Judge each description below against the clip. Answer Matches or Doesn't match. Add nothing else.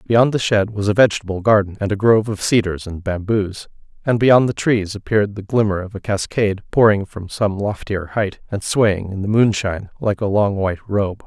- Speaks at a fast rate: Matches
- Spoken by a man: Matches